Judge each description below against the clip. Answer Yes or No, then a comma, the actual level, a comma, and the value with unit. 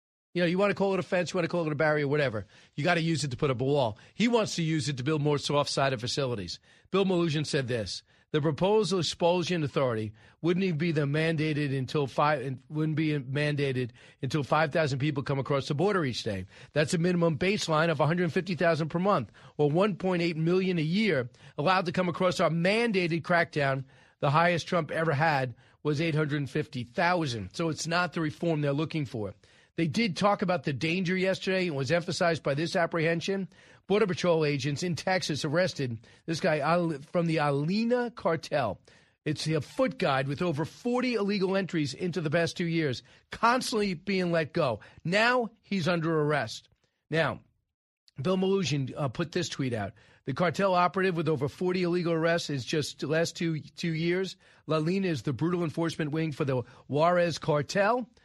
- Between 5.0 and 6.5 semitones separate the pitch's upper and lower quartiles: No, average, 3.7 semitones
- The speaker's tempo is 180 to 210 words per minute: Yes, average, 185 wpm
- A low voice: No, medium, 165 Hz